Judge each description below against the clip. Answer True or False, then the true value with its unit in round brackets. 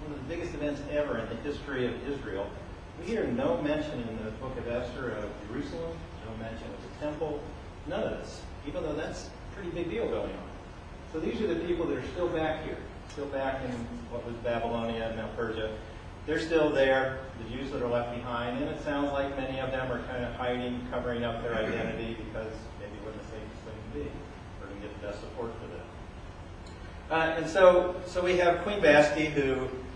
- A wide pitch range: False (4.7 semitones)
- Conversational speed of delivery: False (210 wpm)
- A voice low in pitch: True (120 Hz)